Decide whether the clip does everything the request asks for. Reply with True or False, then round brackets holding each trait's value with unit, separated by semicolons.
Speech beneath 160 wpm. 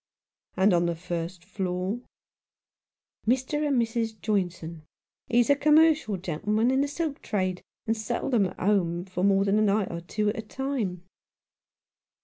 False (165 wpm)